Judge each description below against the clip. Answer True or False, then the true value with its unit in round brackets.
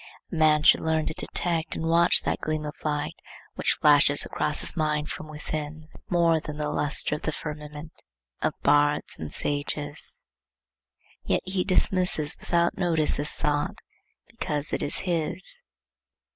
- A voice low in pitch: False (155 Hz)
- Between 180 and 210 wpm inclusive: False (150 wpm)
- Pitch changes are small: True (1.9 semitones)